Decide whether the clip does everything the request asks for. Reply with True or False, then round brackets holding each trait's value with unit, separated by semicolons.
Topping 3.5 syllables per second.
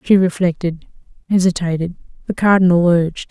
True (5.7 syllables/s)